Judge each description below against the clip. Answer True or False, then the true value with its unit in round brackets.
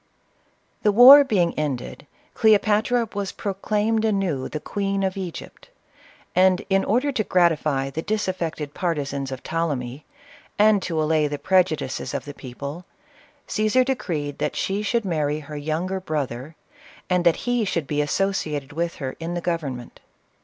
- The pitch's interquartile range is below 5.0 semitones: False (5.4 semitones)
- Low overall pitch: False (170 Hz)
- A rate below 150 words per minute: False (155 wpm)